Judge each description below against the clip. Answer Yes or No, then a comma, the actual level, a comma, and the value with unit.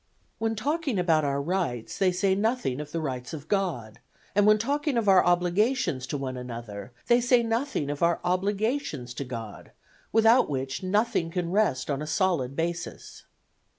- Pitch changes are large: Yes, wide, 7.8 semitones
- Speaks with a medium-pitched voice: Yes, medium, 175 Hz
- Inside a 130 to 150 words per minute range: No, average, 170 wpm